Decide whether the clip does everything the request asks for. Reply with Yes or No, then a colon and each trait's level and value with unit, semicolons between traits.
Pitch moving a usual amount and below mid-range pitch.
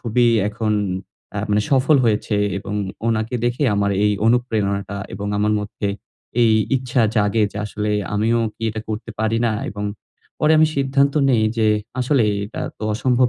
Yes: average, 3.0 semitones; low, 110 Hz